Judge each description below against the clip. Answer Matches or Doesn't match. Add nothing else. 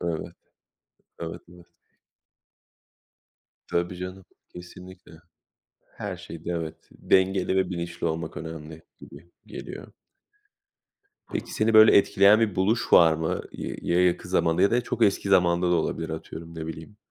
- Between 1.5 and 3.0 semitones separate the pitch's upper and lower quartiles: Matches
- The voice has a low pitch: Matches